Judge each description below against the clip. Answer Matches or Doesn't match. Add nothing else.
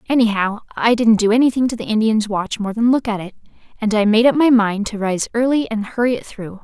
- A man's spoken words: Doesn't match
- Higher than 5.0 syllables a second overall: Matches